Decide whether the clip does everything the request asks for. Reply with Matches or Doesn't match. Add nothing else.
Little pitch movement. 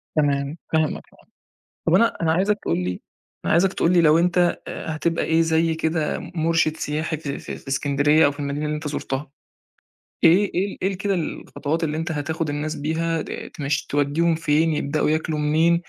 Matches